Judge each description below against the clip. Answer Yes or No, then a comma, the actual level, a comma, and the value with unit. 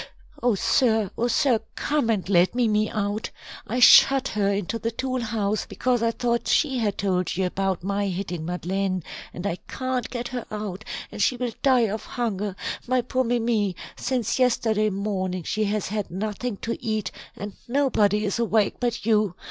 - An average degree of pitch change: Yes, average, 3.3 semitones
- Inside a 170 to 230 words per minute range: Yes, average, 175 wpm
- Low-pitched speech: No, high, 215 Hz